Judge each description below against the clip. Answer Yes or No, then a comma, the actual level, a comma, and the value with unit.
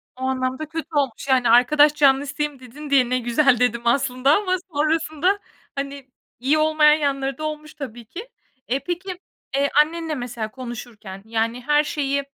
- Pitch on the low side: No, very high, 275 Hz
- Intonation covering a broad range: No, average, 3.4 semitones